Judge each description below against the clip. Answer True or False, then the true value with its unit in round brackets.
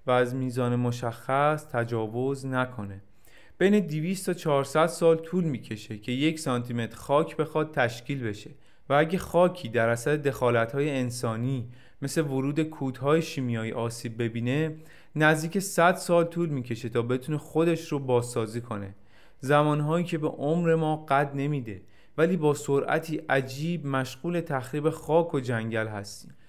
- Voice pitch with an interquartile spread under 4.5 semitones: False (4.8 semitones)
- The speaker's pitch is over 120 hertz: True (140 Hz)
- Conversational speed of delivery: True (140 wpm)